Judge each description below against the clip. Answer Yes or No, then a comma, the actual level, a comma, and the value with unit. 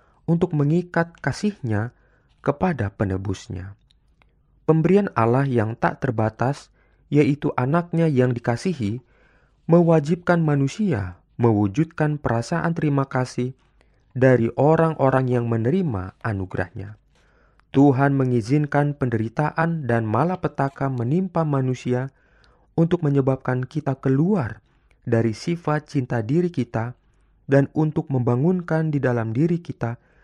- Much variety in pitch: No, average, 5.0 semitones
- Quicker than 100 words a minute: No, average, 95 wpm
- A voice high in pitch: No, low, 135 Hz